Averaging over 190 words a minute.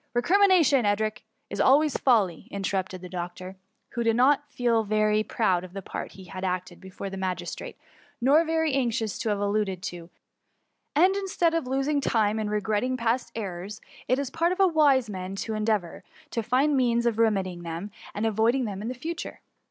Yes: fast, 205 wpm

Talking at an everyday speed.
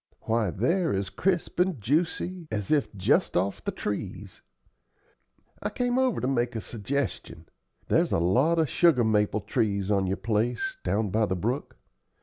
Yes: average, 160 wpm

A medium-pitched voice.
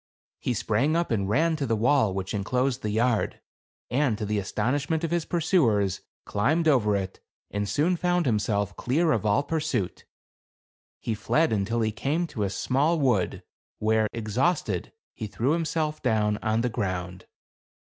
No: low, 115 Hz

